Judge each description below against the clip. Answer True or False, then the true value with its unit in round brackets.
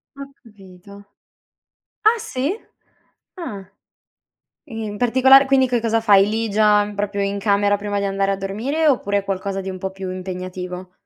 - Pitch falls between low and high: False (205 Hz)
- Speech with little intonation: False (3.6 semitones)